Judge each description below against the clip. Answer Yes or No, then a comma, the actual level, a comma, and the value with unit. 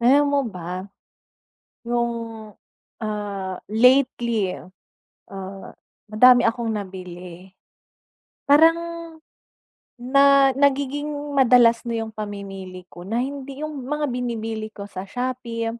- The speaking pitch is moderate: No, high, 230 Hz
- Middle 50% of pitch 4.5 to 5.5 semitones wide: Yes, average, 4.8 semitones